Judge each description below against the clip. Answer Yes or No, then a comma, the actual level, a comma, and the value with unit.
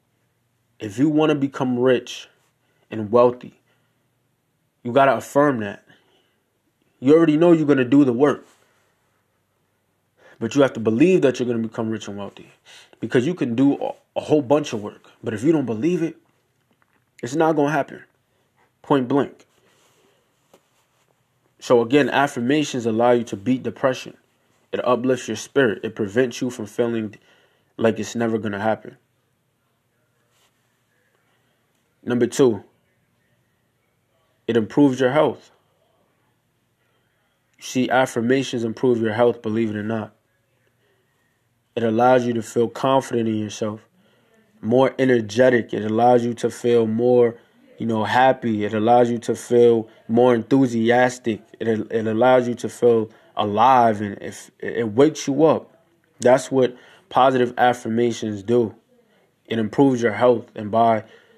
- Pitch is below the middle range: Yes, low, 120 Hz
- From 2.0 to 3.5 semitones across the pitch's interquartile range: Yes, narrow, 2.4 semitones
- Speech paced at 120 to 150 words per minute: Yes, average, 140 wpm